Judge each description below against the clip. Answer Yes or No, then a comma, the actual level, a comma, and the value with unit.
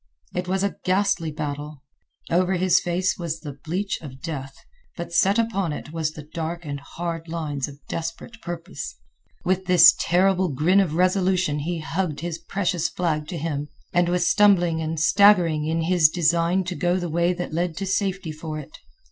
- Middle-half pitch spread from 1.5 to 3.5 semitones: Yes, average, 2.8 semitones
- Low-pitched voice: No, medium, 170 Hz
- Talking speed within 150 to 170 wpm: No, average, 180 wpm